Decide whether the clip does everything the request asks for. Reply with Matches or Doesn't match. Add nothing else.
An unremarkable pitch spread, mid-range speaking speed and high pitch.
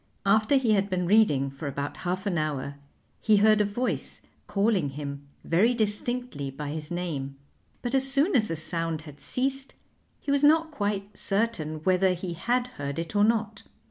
Doesn't match